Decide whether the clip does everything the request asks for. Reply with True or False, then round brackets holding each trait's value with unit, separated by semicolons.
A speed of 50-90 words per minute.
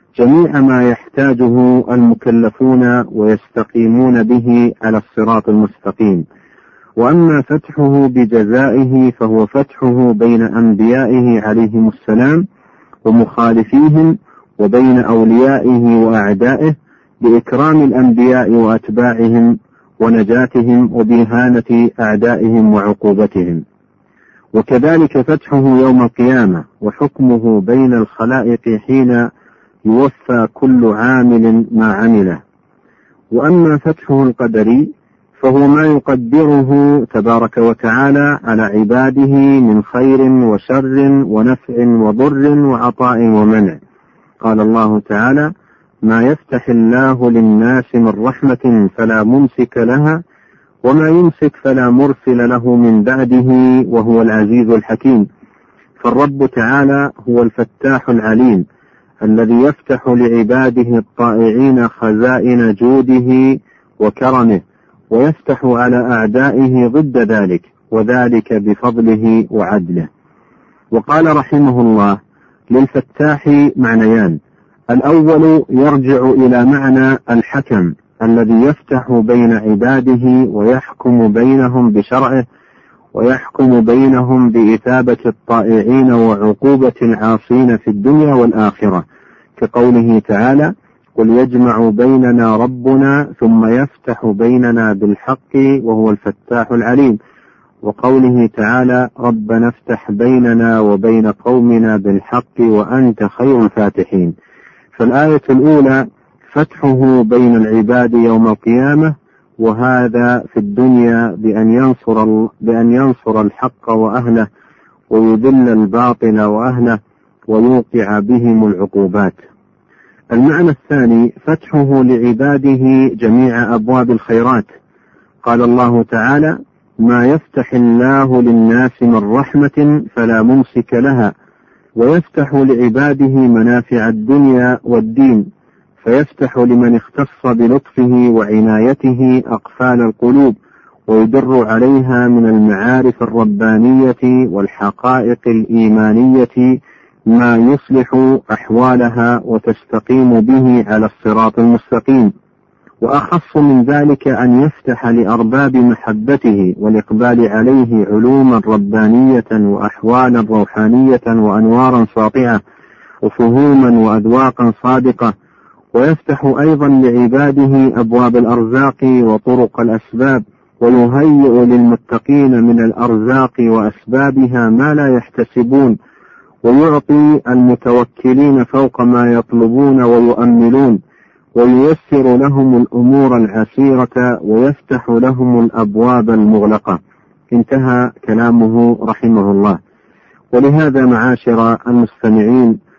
True (85 wpm)